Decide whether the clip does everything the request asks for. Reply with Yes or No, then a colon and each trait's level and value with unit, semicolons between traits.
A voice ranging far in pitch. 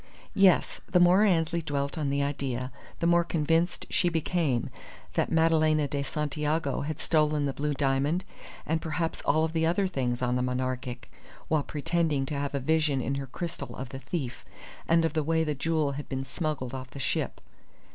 No: average, 3.2 semitones